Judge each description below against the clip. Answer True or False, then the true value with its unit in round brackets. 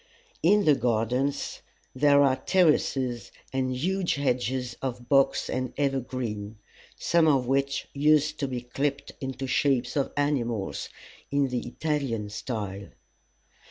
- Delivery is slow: True (125 wpm)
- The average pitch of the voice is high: False (135 Hz)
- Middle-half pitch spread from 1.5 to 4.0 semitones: True (2.7 semitones)